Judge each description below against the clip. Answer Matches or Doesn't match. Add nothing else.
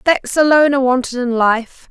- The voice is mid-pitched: Doesn't match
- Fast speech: Doesn't match